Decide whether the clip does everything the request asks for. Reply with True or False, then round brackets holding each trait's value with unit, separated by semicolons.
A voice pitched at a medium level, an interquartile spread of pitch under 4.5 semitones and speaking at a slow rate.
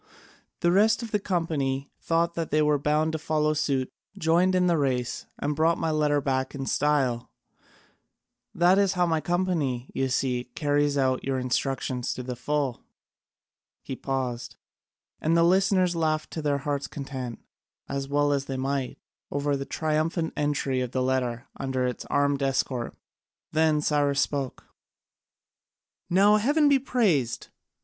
False (145 Hz; 3.7 semitones; 150 wpm)